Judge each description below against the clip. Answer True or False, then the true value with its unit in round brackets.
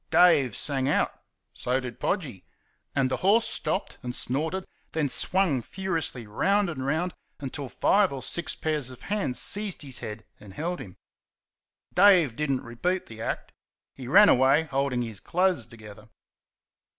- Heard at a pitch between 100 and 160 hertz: True (140 Hz)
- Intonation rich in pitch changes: True (6.3 semitones)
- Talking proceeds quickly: False (155 wpm)